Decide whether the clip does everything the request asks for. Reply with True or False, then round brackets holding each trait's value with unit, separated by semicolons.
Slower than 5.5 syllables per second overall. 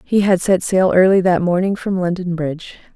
True (5.2 syllables/s)